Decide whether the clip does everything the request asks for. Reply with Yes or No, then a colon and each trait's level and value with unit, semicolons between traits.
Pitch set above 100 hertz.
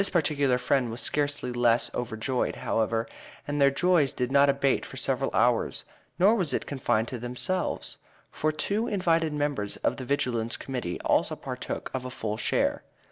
Yes: low, 135 Hz